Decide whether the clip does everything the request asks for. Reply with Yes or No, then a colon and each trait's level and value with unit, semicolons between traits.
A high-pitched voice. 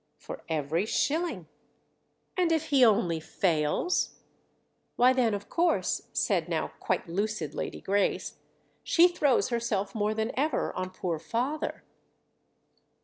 Yes: high, 220 Hz